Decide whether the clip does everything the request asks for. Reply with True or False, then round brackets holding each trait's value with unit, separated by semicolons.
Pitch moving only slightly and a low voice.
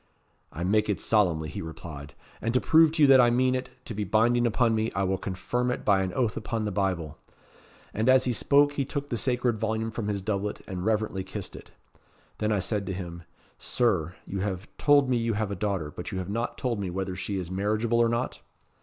False (4.0 semitones; 105 Hz)